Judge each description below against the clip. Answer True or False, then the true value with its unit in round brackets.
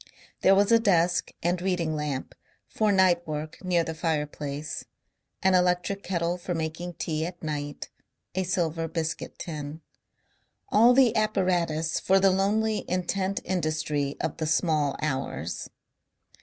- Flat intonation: False (3.3 semitones)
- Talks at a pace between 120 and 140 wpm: True (135 wpm)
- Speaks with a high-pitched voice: False (170 Hz)